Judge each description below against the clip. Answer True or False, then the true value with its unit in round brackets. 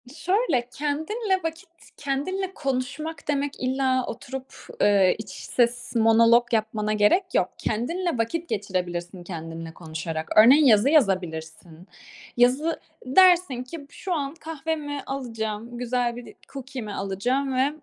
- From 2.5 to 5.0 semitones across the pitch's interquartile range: False (5.6 semitones)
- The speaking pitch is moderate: False (250 Hz)